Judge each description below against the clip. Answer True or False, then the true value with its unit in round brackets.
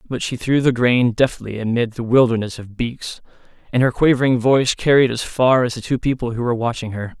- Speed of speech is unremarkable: False (215 wpm)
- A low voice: True (120 Hz)